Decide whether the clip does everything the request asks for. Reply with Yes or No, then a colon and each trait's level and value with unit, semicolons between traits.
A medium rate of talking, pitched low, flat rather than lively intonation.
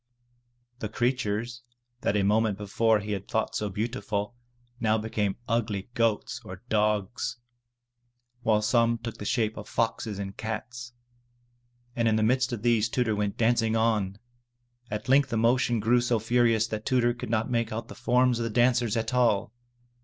Yes: average, 170 wpm; low, 110 Hz; narrow, 2.1 semitones